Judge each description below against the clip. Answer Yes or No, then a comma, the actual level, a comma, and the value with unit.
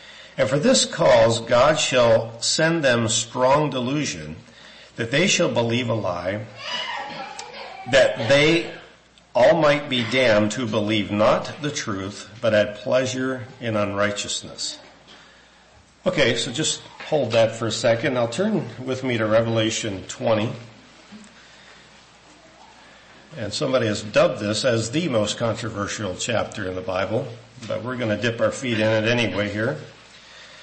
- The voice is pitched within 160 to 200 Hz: No, low, 115 Hz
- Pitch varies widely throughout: No, average, 3.3 semitones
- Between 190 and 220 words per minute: No, average, 140 wpm